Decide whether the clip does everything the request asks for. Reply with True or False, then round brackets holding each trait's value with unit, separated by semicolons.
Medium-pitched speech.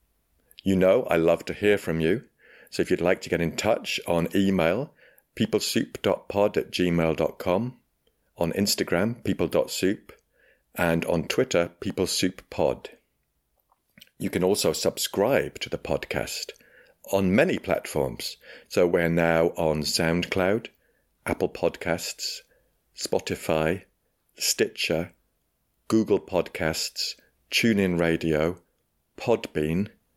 False (85 Hz)